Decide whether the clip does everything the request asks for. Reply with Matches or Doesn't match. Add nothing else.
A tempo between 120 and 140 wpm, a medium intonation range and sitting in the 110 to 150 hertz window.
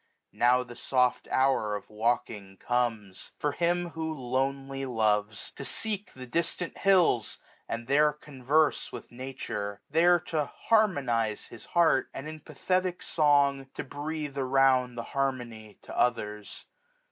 Matches